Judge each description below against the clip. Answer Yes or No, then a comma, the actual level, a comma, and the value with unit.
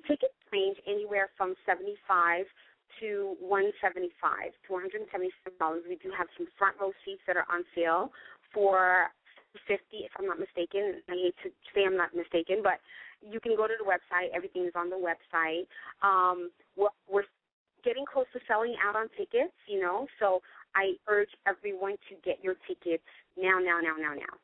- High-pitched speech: Yes, high, 195 Hz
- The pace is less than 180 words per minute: Yes, average, 170 wpm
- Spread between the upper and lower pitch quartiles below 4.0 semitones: Yes, average, 3.4 semitones